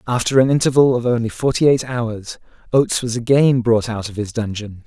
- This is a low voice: Yes, low, 120 Hz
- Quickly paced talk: No, average, 195 wpm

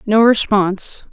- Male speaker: No, female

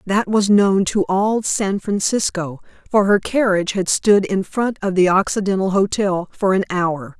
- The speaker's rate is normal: Yes, average, 175 wpm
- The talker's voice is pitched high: Yes, high, 195 Hz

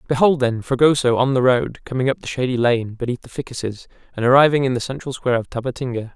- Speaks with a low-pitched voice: Yes, low, 130 Hz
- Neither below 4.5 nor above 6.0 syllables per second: No, 6.5 syllables/s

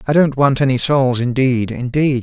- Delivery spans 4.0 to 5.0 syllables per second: Yes, 4.7 syllables/s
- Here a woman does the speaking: No, male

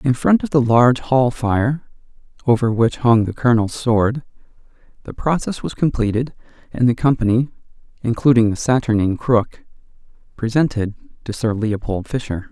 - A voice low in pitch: Yes, low, 120 Hz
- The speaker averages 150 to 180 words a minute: No, average, 140 wpm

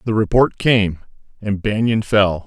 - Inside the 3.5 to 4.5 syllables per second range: Yes, 4.1 syllables/s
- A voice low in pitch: Yes, low, 105 Hz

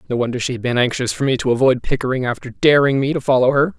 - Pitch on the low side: Yes, low, 125 Hz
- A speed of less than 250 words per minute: No, fast, 270 wpm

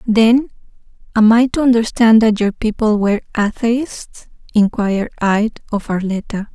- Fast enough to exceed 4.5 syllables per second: No, 4.4 syllables/s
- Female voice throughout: Yes, female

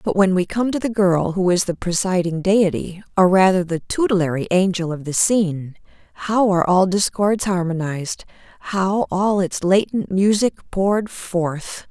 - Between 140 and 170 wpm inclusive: Yes, average, 160 wpm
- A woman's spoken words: Yes, female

